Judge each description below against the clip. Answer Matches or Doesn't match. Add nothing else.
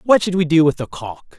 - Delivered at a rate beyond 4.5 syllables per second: Matches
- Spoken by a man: Matches